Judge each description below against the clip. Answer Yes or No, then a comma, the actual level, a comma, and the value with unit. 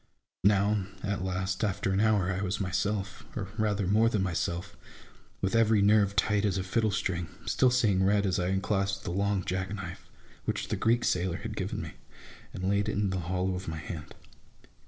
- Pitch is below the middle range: Yes, very low, 95 Hz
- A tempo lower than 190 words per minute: No, average, 195 wpm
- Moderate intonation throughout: No, narrow, 1.9 semitones